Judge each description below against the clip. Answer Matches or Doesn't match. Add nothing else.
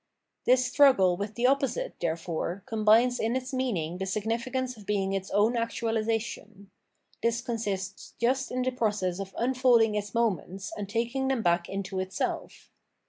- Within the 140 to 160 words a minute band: Matches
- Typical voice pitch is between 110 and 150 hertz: Doesn't match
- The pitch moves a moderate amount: Matches